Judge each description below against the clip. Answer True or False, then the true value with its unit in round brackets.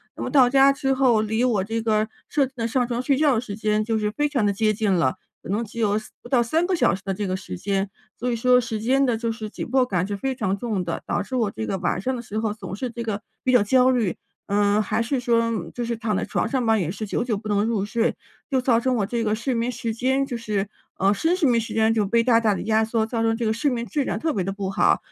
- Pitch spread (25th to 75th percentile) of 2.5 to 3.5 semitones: True (3.1 semitones)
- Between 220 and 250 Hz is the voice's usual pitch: True (225 Hz)